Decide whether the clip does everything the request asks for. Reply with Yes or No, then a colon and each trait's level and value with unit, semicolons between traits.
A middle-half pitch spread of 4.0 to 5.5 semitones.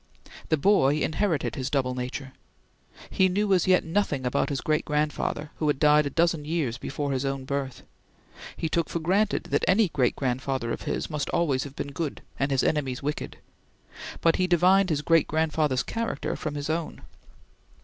No: average, 3.6 semitones